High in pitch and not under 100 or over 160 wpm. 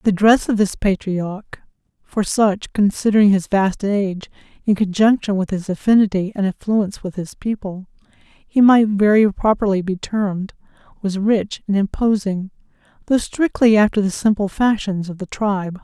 Yes: high, 205 Hz; average, 145 wpm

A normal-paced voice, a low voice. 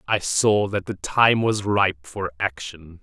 Yes: average, 180 wpm; very low, 95 Hz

